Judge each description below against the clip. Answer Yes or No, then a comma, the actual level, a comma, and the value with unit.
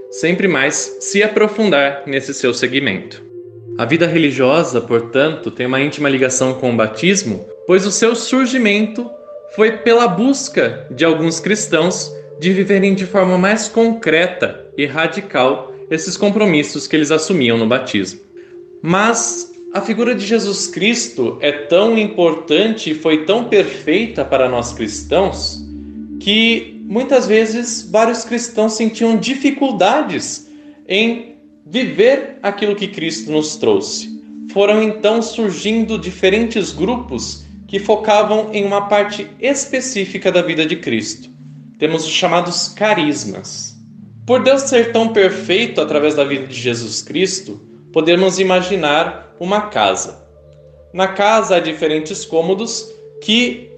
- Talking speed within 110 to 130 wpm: Yes, average, 125 wpm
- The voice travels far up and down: Yes, wide, 7.3 semitones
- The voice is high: Yes, high, 195 Hz